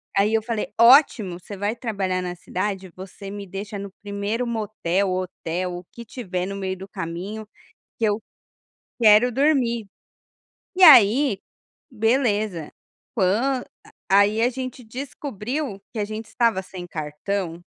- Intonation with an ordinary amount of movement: Yes, average, 3.7 semitones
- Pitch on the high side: Yes, high, 205 Hz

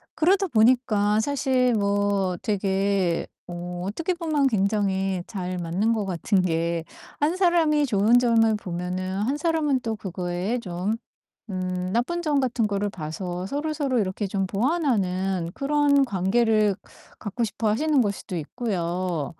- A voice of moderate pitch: No, high, 205 Hz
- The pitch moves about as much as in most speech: No, wide, 5.8 semitones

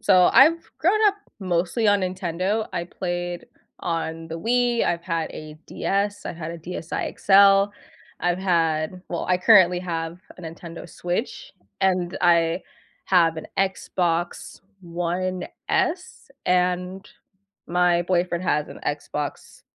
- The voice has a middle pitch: Yes, medium, 180 Hz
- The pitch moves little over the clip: Yes, narrow, 2.3 semitones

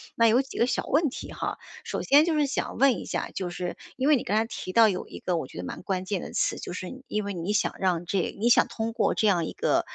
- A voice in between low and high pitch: No, high, 210 Hz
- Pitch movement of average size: No, wide, 5.8 semitones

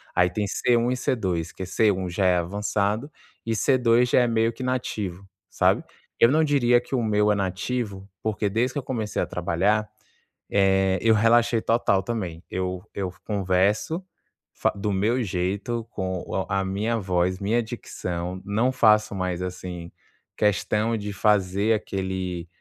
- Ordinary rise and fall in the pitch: Yes, average, 3.6 semitones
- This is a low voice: Yes, low, 105 Hz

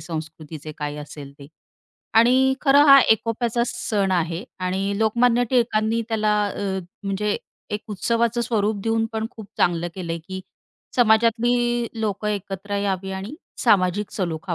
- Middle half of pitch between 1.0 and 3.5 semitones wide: No, average, 3.9 semitones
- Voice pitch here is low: No, high, 210 Hz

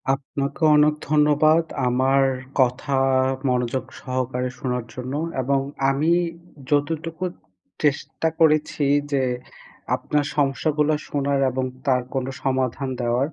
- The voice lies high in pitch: No, medium, 140 Hz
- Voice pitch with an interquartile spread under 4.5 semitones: Yes, narrow, 2.6 semitones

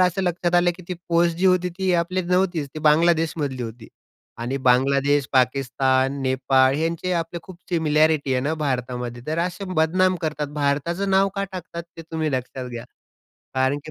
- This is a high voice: No, medium, 155 Hz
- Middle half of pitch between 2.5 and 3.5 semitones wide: No, average, 4.8 semitones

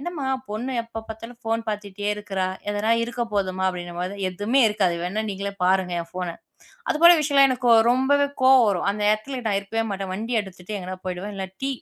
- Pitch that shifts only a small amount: No, average, 4.2 semitones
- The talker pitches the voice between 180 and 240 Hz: Yes, high, 210 Hz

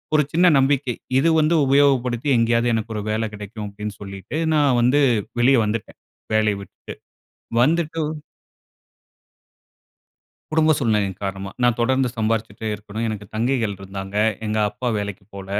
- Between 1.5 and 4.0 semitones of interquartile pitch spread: No, average, 4.5 semitones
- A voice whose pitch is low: Yes, low, 115 Hz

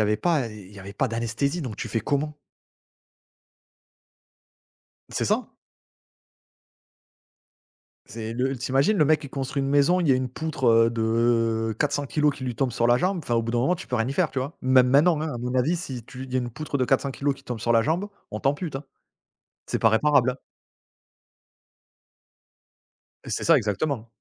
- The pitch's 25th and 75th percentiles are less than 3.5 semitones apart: No, average, 3.8 semitones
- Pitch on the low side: Yes, low, 130 Hz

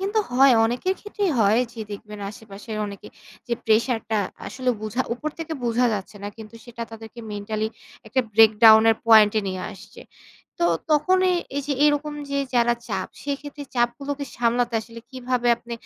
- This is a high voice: Yes, high, 235 Hz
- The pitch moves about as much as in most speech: Yes, average, 4.2 semitones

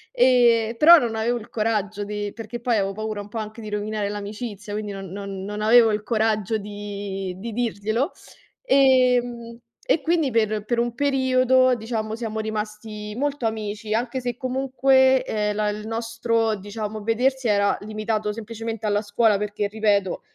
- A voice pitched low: No, high, 220 Hz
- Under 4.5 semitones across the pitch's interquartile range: Yes, narrow, 2.5 semitones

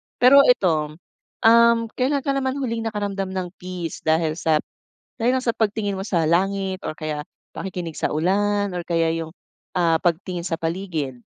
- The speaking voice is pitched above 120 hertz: Yes, medium, 185 Hz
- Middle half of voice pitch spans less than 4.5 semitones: No, average, 4.9 semitones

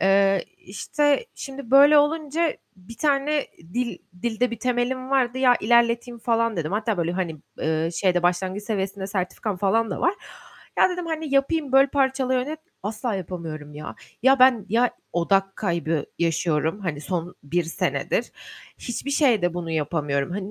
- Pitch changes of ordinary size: No, wide, 7.0 semitones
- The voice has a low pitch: No, high, 220 Hz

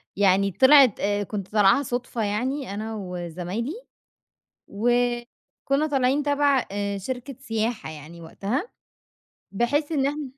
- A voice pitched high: Yes, high, 235 Hz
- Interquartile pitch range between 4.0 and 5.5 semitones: Yes, average, 5.2 semitones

